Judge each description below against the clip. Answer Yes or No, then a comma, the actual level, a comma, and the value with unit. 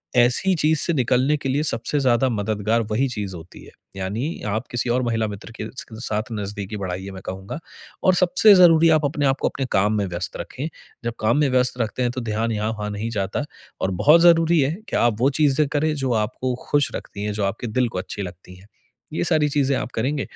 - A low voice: Yes, low, 120 Hz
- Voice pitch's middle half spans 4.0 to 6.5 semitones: Yes, wide, 5.4 semitones